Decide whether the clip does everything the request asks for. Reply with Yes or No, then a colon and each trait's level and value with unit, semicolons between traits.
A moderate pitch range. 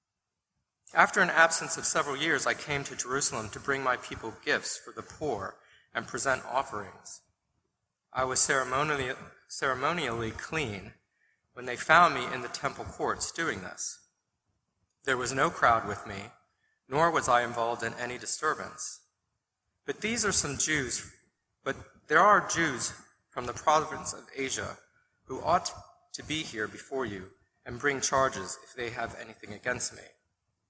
Yes: average, 4.0 semitones